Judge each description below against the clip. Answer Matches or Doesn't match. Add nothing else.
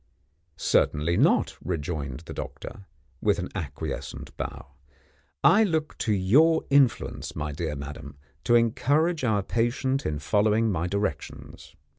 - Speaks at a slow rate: Matches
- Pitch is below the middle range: Matches